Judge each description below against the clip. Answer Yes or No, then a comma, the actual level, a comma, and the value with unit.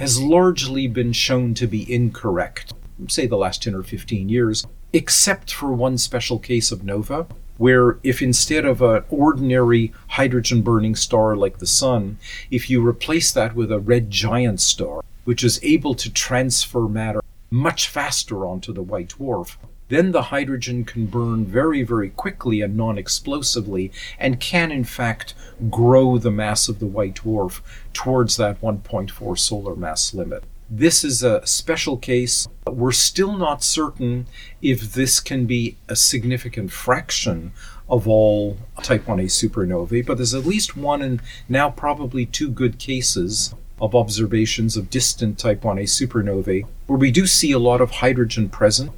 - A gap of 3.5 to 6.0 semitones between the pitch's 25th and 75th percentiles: No, average, 3.1 semitones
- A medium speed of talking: Yes, average, 160 wpm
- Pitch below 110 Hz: No, low, 120 Hz